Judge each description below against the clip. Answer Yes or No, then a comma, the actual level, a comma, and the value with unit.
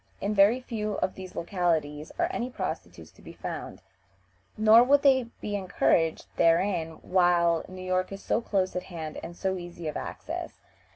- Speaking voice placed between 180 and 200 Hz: Yes, medium, 185 Hz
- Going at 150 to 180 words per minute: Yes, average, 170 wpm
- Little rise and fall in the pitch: No, average, 3.8 semitones